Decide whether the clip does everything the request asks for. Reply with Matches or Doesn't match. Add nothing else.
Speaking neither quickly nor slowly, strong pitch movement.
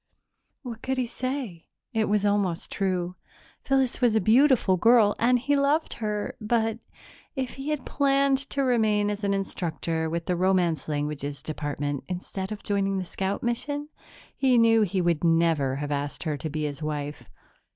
Matches